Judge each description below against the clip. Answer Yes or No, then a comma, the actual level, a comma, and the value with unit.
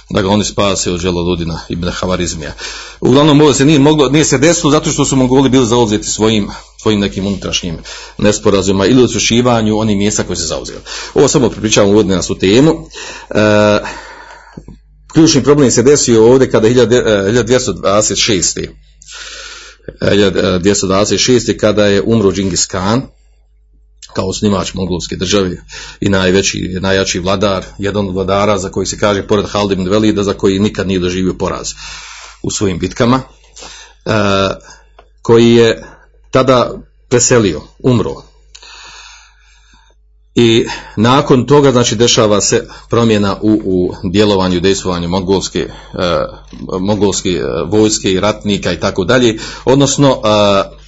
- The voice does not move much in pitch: No, average, 3.9 semitones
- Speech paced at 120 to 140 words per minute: Yes, average, 125 wpm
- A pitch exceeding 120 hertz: No, low, 105 Hz